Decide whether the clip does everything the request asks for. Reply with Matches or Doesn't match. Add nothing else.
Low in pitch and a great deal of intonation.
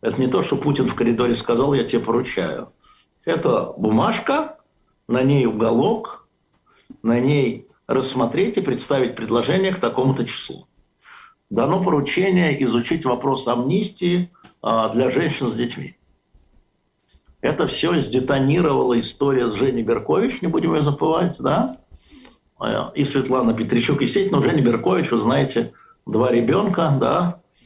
Matches